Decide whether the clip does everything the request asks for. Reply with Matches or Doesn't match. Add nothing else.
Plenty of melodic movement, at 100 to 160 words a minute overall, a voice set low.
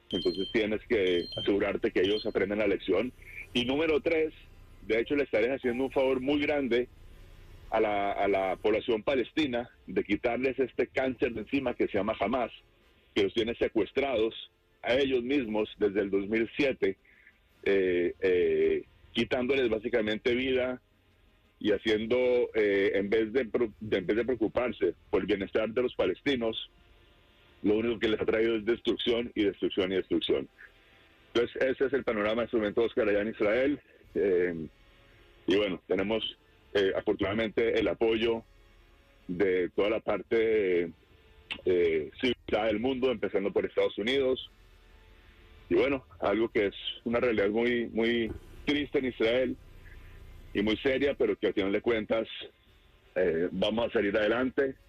Matches